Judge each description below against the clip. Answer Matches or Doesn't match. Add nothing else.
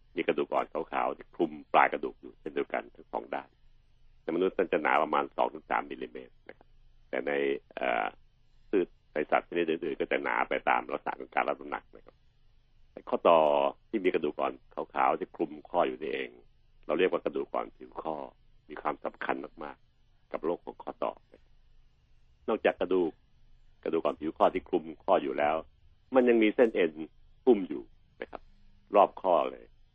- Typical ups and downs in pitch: Doesn't match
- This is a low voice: Matches